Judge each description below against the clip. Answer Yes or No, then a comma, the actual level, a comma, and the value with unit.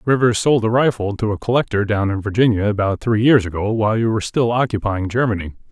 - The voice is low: Yes, low, 110 Hz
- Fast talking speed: Yes, fast, 210 wpm